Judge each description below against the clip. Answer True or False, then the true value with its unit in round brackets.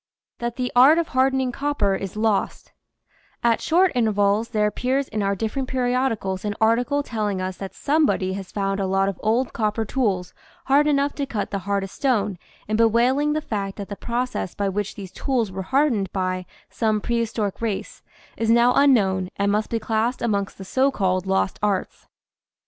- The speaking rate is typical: True (180 wpm)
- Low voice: False (220 Hz)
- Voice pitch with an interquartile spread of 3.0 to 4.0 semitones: False (4.4 semitones)